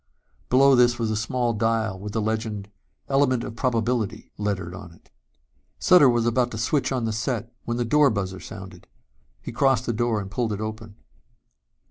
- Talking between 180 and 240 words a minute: Yes, average, 185 wpm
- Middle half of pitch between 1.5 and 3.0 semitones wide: Yes, narrow, 2.6 semitones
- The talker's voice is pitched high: No, low, 115 Hz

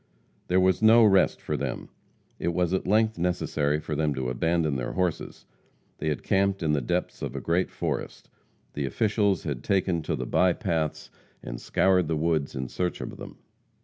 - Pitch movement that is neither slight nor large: Yes, average, 3.8 semitones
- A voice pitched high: No, very low, 85 Hz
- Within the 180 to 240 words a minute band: Yes, average, 185 wpm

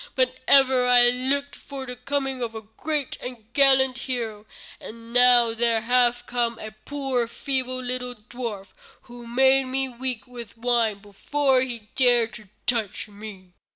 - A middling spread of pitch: No, narrow, 2.3 semitones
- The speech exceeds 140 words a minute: Yes, average, 155 wpm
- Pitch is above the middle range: Yes, high, 245 Hz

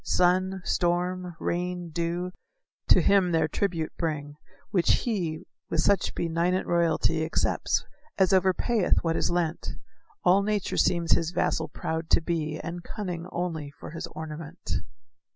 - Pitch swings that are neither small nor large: No, narrow, 2.0 semitones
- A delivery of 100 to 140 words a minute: Yes, slow, 135 wpm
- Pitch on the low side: No, medium, 175 Hz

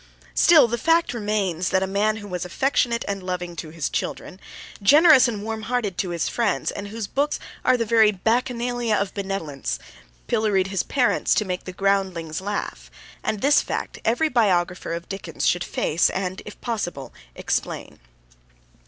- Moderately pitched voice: No, high, 205 Hz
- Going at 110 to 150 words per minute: No, average, 165 wpm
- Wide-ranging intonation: No, average, 4.4 semitones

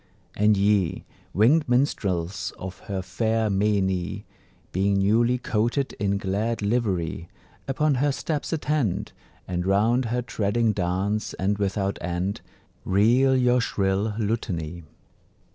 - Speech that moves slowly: Yes, slow, 115 wpm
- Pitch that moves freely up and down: No, average, 3.6 semitones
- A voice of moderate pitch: No, low, 105 Hz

